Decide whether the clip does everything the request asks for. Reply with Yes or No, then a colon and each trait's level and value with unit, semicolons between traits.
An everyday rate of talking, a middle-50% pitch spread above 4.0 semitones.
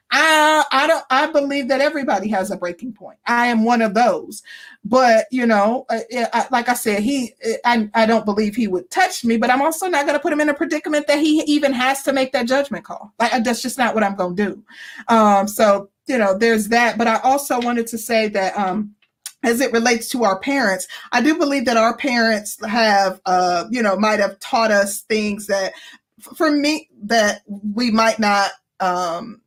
No: fast, 220 wpm; average, 4.4 semitones